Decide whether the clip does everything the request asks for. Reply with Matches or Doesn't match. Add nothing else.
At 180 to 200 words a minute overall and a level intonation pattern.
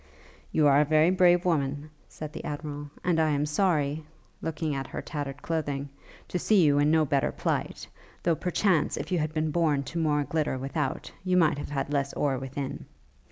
Matches